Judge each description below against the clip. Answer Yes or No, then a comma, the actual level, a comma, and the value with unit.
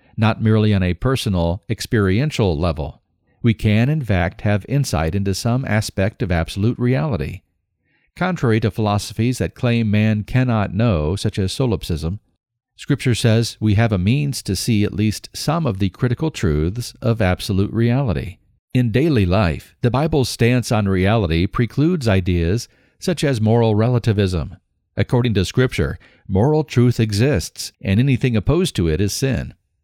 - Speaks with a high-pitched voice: No, low, 110 Hz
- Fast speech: No, average, 150 wpm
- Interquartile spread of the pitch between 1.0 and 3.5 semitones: No, average, 4.2 semitones